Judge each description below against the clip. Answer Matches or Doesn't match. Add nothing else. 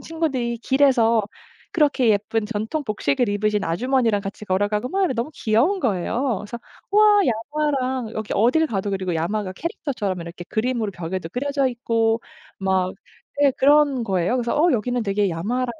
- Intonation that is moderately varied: Matches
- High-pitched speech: Matches